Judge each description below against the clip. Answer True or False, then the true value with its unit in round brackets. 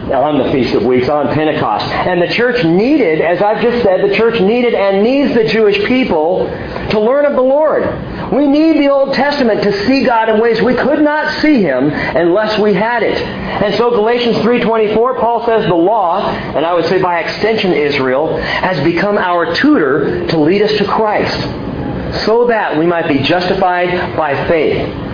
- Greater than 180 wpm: True (190 wpm)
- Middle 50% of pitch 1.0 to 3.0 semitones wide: False (5.3 semitones)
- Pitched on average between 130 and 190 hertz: False (215 Hz)